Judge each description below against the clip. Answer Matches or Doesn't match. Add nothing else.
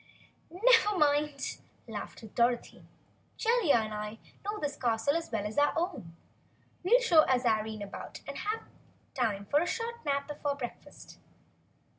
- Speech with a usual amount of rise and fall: Doesn't match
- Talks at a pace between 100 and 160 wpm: Matches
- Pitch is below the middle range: Doesn't match